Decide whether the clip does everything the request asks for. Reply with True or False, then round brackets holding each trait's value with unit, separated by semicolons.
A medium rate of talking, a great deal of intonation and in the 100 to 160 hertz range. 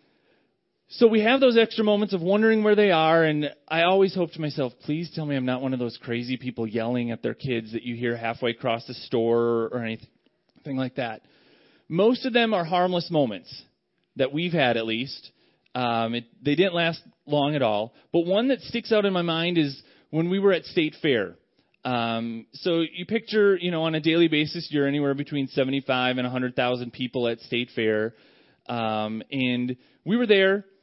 True (195 wpm; 6.7 semitones; 140 Hz)